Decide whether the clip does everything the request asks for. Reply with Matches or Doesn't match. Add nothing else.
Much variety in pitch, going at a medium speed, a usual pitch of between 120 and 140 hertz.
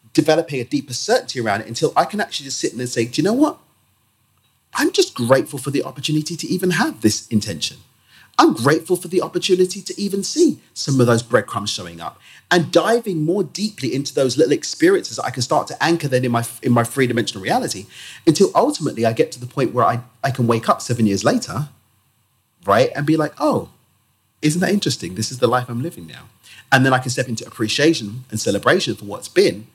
Doesn't match